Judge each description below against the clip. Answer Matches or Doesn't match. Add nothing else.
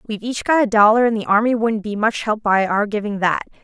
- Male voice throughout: Doesn't match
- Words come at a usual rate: Doesn't match